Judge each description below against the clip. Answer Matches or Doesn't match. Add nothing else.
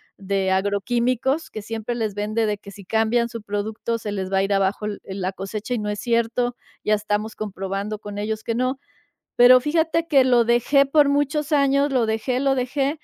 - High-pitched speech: Matches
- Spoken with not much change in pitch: Doesn't match